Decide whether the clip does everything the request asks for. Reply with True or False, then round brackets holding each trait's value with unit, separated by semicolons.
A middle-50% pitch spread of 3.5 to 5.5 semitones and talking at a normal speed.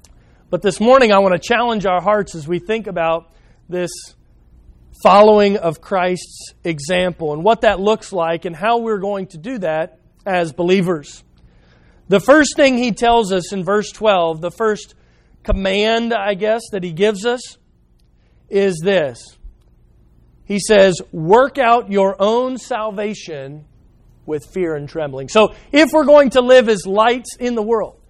True (5.1 semitones; 160 wpm)